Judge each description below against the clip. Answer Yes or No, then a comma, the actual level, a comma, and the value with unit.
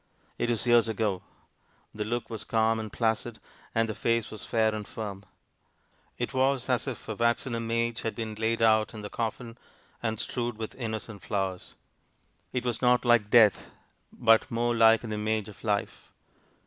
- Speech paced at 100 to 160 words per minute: No, average, 175 wpm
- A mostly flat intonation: Yes, narrow, 1.5 semitones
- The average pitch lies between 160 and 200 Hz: No, low, 115 Hz